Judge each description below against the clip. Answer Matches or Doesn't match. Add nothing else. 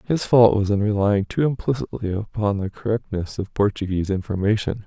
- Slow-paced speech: Doesn't match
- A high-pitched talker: Doesn't match